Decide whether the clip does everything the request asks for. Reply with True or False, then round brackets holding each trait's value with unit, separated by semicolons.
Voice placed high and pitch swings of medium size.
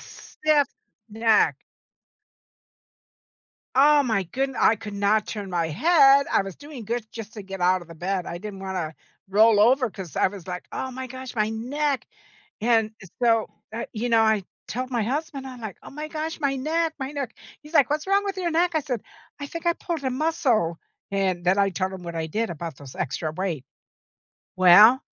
False (225 Hz; 6.4 semitones)